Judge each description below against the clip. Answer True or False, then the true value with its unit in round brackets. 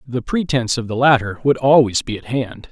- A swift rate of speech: True (220 wpm)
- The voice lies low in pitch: True (125 Hz)